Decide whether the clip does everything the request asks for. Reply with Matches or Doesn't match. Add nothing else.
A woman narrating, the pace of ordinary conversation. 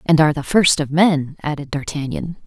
Matches